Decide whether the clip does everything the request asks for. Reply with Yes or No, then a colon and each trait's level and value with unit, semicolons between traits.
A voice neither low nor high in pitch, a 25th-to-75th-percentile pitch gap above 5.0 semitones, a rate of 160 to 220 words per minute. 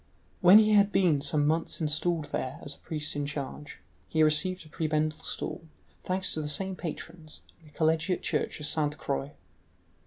No: medium, 155 Hz; average, 2.9 semitones; average, 180 wpm